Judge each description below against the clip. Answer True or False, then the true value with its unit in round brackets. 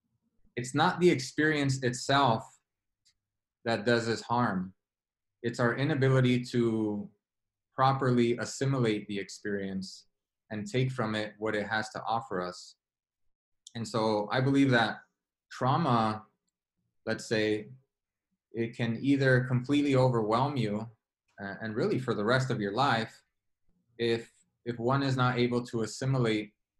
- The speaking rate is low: True (130 wpm)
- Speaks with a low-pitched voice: True (115 Hz)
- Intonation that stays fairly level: False (3.5 semitones)